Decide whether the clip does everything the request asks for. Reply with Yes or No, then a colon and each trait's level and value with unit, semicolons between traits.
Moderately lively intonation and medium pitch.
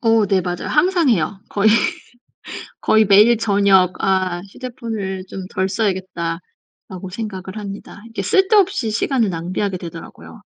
No: average, 3.3 semitones; high, 200 Hz